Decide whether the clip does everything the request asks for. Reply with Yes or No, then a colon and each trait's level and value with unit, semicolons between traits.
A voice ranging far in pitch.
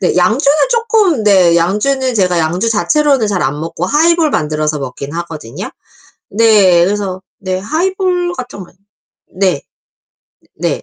Yes: wide, 8.7 semitones